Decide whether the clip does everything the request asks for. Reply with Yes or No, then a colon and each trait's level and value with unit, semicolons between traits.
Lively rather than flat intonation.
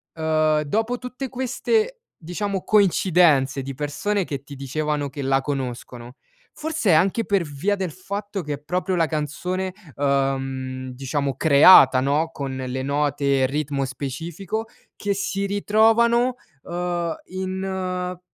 Yes: wide, 6.0 semitones